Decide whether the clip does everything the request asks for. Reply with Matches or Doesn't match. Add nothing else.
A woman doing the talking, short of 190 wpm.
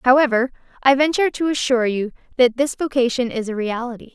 Matches